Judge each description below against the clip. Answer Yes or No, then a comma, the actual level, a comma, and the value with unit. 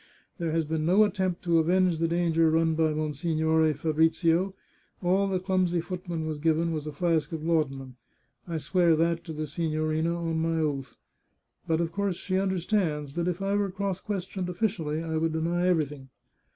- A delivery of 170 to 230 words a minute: Yes, average, 180 wpm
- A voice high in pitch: No, medium, 165 Hz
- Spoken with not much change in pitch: Yes, narrow, 2.3 semitones